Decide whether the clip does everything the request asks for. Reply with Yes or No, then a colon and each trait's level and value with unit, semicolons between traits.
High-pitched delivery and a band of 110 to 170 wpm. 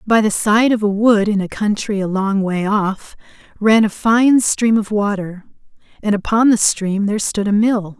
No: high, 210 Hz; fast, 205 wpm